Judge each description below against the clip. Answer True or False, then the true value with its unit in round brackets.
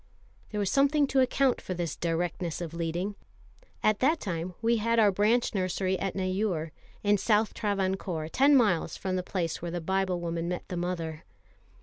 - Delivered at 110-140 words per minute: False (175 wpm)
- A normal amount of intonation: True (3.8 semitones)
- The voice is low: False (185 Hz)